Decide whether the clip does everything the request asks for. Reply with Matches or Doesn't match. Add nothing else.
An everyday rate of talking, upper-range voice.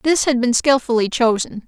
Matches